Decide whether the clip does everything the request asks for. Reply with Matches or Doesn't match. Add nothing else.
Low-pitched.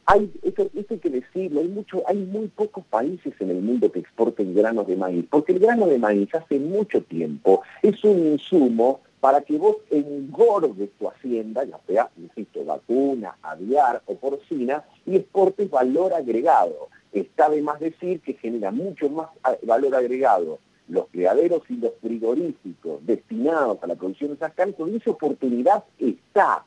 Doesn't match